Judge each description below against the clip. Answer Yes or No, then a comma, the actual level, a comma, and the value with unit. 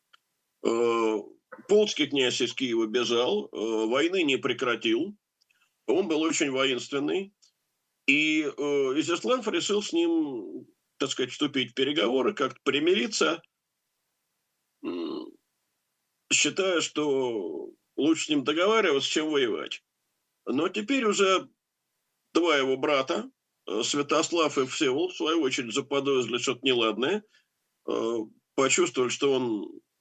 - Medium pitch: No, high, 205 Hz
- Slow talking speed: Yes, slow, 100 wpm